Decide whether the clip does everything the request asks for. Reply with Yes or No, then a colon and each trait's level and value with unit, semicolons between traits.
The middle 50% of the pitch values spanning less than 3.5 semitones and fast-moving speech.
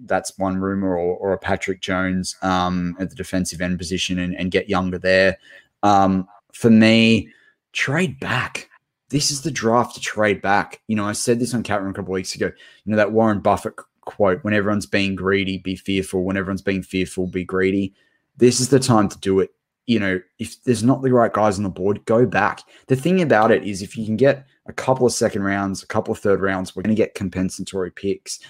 Yes: average, 2.9 semitones; fast, 225 wpm